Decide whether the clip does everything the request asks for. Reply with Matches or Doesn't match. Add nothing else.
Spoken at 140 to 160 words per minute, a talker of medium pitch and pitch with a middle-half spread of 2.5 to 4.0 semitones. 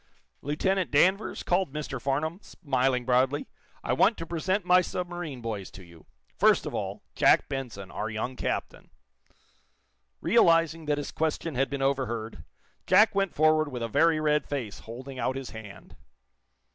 Doesn't match